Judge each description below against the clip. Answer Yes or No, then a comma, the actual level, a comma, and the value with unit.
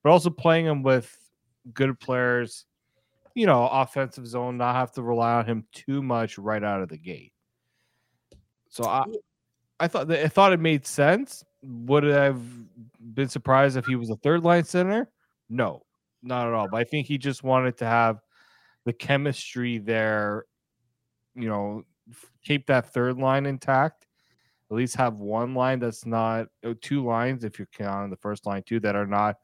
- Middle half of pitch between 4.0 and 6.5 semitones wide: No, average, 3.1 semitones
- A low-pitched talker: Yes, low, 125 Hz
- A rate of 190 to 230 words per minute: No, average, 175 wpm